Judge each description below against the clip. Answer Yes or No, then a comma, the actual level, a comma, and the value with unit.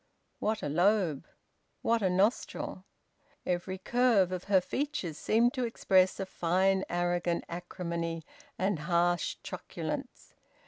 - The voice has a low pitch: No, medium, 185 Hz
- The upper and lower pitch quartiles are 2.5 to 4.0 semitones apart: Yes, average, 2.9 semitones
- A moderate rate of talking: No, slow, 120 wpm